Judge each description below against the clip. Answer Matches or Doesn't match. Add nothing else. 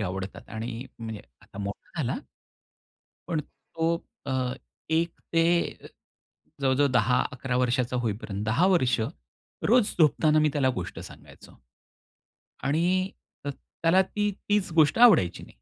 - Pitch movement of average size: Doesn't match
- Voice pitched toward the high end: Doesn't match